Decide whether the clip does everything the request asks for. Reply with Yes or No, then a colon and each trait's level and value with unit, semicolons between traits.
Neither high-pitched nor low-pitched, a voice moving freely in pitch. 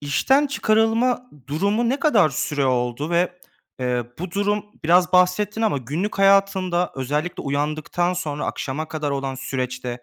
Yes: medium, 175 Hz; wide, 6.4 semitones